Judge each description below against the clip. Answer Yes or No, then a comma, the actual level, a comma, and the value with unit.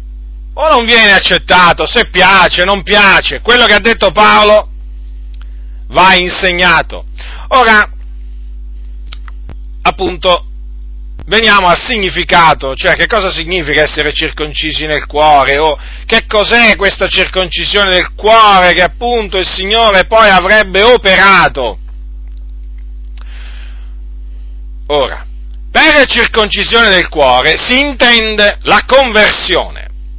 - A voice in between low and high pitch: Yes, medium, 175 Hz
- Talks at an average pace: No, slow, 100 wpm